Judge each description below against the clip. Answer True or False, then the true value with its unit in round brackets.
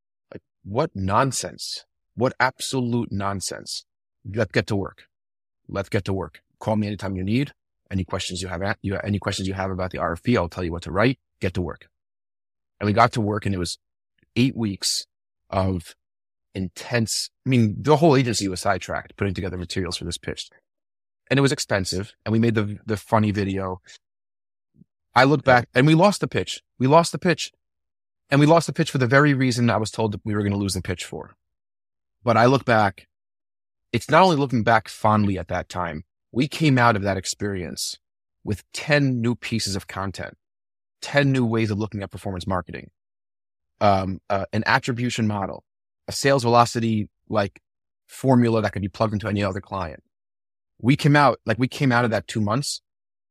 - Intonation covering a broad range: False (4.2 semitones)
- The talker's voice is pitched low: True (105 Hz)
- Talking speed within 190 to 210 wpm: True (195 wpm)